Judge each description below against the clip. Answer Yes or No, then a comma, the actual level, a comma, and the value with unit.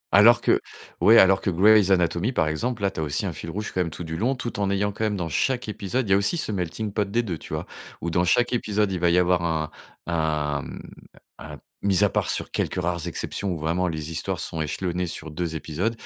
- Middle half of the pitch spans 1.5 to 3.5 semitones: No, average, 4.0 semitones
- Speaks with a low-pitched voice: Yes, very low, 90 Hz